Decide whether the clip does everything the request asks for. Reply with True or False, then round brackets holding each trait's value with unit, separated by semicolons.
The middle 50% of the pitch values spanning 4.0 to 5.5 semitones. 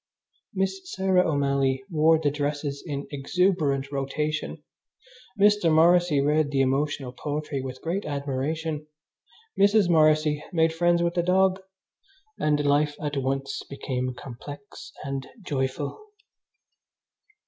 False (3.6 semitones)